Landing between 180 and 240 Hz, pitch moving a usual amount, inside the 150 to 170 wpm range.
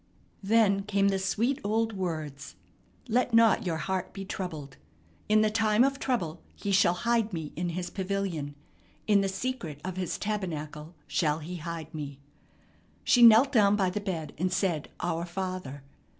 Yes: high, 190 Hz; average, 4.4 semitones; average, 165 wpm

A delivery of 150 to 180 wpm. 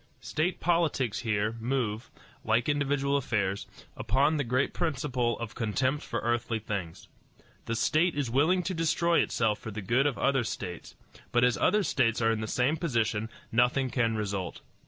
Yes: average, 165 wpm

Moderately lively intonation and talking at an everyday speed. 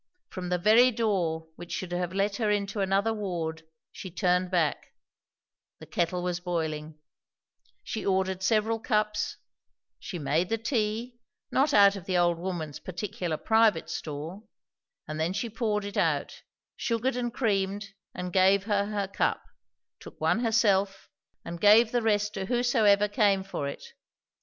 Yes: average, 3.4 semitones; average, 150 wpm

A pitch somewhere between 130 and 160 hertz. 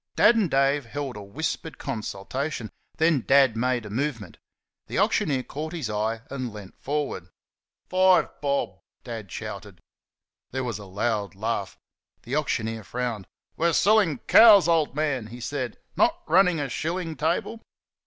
Yes: low, 135 Hz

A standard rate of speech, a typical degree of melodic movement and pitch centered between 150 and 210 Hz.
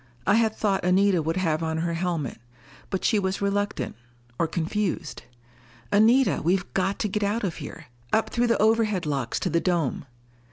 Yes: average, 175 wpm; average, 4.0 semitones; high, 190 Hz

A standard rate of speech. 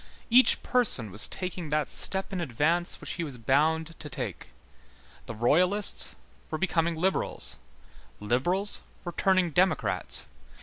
No: slow, 130 wpm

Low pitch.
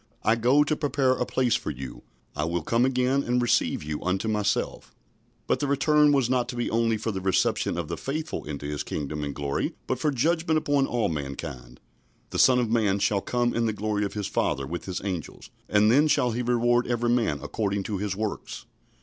Yes: low, 115 Hz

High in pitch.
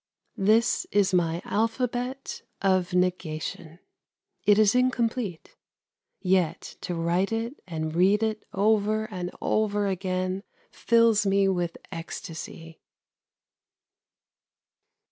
Yes: high, 195 Hz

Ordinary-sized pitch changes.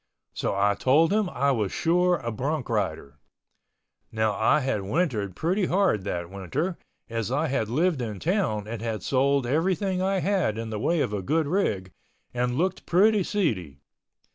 No: wide, 8.7 semitones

